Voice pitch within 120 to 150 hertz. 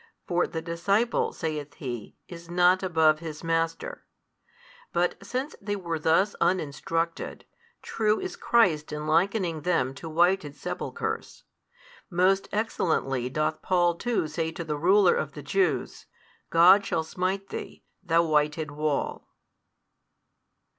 No: medium, 170 Hz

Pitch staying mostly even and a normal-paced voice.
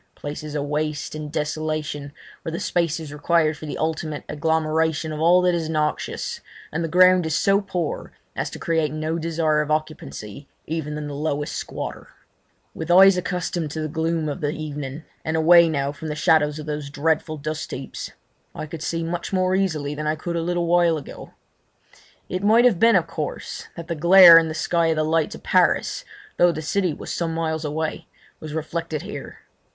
Yes: narrow, 1.9 semitones; average, 195 wpm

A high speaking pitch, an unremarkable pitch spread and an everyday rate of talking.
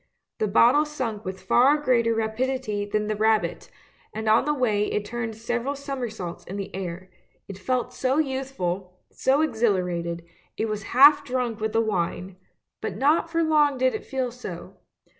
Yes: high, 230 Hz; average, 4.4 semitones; average, 175 wpm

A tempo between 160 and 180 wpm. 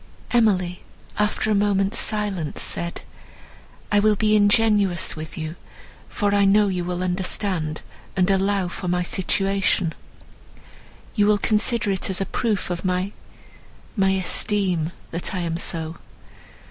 No: slow, 135 wpm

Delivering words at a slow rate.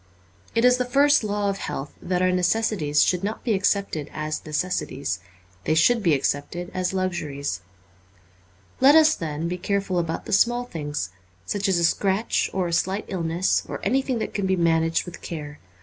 No: average, 180 wpm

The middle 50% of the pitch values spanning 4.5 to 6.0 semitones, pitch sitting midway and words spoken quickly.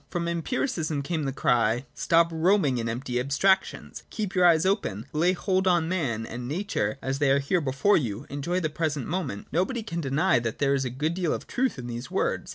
Yes: average, 5.3 semitones; medium, 155 Hz; fast, 215 wpm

